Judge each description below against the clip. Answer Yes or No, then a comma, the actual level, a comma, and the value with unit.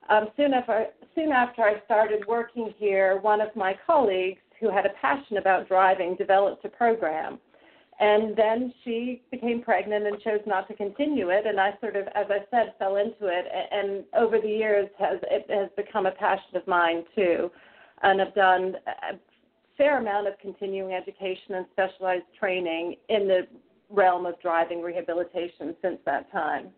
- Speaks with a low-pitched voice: No, high, 200 Hz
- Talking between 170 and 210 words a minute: Yes, average, 175 wpm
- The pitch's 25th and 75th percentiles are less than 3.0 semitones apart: Yes, narrow, 2.5 semitones